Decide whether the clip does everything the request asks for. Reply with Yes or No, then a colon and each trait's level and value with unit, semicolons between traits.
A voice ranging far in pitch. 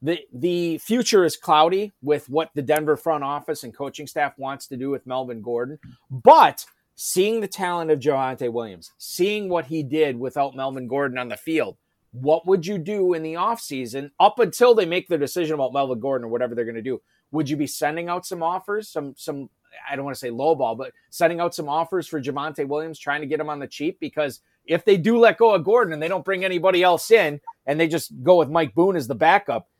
No: average, 4.6 semitones